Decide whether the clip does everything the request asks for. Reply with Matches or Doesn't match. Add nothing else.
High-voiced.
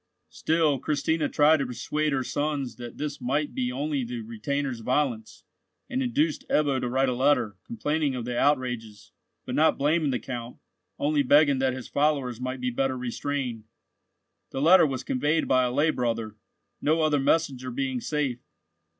Doesn't match